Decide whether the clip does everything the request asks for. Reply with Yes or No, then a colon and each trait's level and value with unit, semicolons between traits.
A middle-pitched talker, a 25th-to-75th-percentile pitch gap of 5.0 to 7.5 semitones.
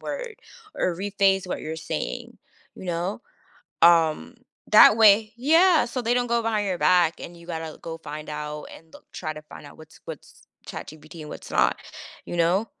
Yes: medium, 175 Hz; wide, 5.4 semitones